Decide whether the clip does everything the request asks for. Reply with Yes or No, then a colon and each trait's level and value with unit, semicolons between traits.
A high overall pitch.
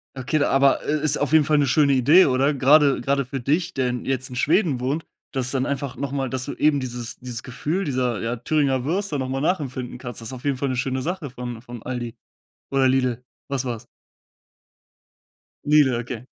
No: low, 135 Hz